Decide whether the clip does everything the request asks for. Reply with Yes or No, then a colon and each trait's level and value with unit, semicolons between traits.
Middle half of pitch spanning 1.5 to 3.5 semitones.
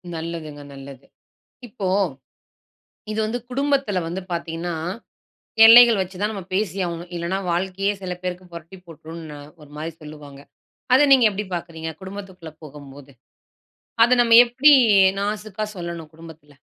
No: average, 4.2 semitones